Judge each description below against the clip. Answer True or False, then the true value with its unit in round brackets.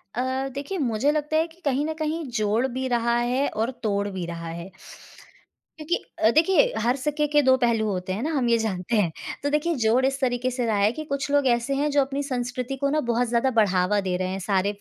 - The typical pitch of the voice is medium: False (245 Hz)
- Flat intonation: False (5.0 semitones)